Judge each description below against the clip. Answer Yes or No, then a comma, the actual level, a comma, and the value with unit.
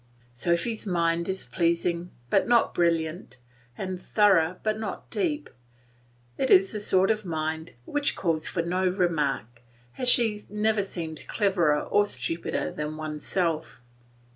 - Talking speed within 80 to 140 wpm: Yes, slow, 135 wpm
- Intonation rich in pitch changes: No, average, 4.2 semitones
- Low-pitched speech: No, medium, 180 Hz